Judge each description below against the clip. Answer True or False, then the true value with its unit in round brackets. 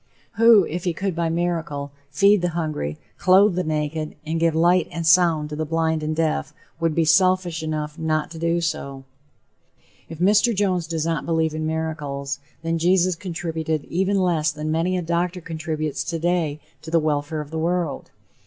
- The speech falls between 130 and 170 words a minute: False (180 wpm)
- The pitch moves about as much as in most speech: False (2.1 semitones)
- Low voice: False (165 Hz)